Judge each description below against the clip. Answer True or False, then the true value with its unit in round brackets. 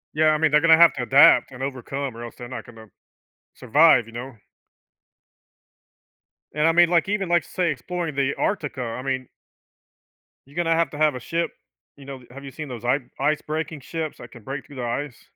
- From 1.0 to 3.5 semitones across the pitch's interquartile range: False (4.0 semitones)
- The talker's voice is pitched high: False (140 Hz)